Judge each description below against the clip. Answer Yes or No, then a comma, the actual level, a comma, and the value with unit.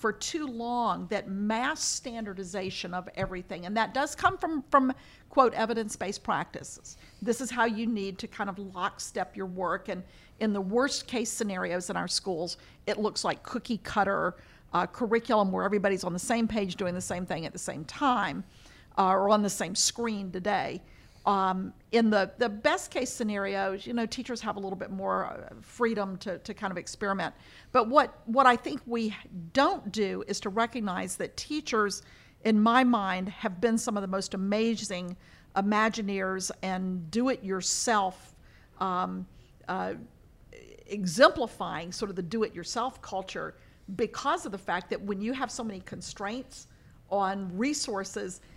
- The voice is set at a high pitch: Yes, high, 205 Hz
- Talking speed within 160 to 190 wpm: Yes, average, 170 wpm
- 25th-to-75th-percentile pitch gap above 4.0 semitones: No, average, 3.6 semitones